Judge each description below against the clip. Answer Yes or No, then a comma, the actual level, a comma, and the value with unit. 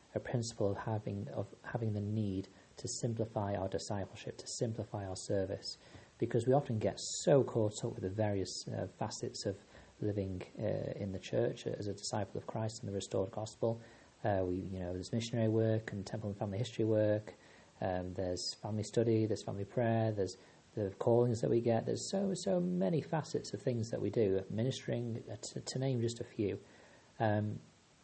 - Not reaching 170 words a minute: No, average, 190 wpm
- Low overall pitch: Yes, low, 110 Hz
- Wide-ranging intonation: No, average, 3.1 semitones